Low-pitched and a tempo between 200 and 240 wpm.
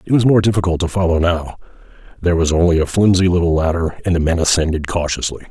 Yes: very low, 85 Hz; fast, 205 wpm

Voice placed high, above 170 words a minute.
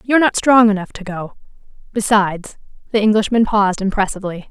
No: high, 210 Hz; average, 145 wpm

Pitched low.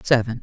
Yes: low, 115 Hz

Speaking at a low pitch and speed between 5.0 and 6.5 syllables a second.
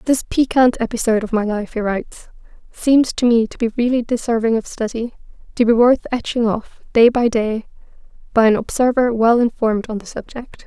No: high, 230 Hz; 5.4 syllables/s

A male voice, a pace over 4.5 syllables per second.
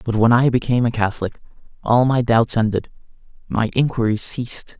Yes: male; 5.7 syllables/s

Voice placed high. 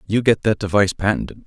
No: low, 100 Hz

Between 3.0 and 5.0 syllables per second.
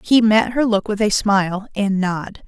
Yes: 4.3 syllables/s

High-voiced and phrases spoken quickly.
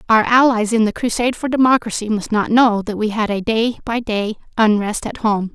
Yes: high, 220 Hz; fast, 215 wpm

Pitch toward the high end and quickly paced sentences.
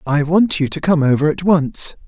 No: medium, 160 Hz; fast, 230 wpm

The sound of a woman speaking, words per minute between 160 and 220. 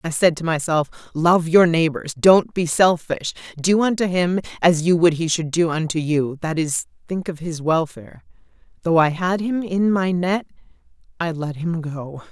Yes: female; average, 180 wpm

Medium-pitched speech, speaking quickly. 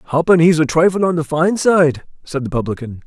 Yes: medium, 155 Hz; fast, 215 wpm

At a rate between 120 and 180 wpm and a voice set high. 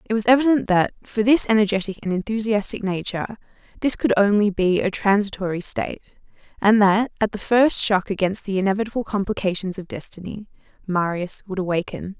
Yes: average, 155 wpm; high, 205 Hz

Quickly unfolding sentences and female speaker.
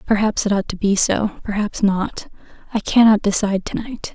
No: average, 190 wpm; female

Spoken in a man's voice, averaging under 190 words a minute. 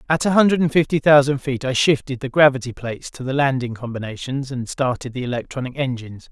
No: male; average, 200 wpm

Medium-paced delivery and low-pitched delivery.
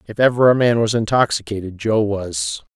Yes: average, 175 wpm; low, 110 Hz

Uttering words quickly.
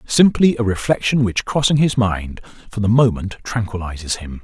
No: average, 160 wpm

